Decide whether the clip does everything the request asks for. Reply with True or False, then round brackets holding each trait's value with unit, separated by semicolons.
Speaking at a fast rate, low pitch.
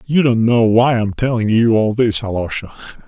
True (215 wpm; 115 Hz)